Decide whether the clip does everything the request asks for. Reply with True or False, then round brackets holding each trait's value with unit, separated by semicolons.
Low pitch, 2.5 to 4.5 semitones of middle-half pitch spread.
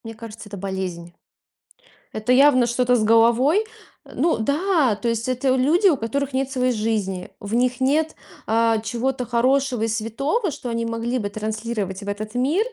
False (235 Hz; 3.4 semitones)